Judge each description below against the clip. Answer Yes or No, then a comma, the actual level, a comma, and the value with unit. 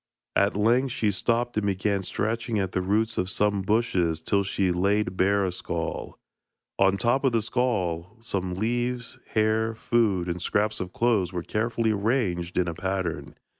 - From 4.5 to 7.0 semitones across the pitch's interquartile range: No, average, 3.7 semitones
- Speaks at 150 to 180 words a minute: Yes, average, 170 wpm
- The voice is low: Yes, low, 100 Hz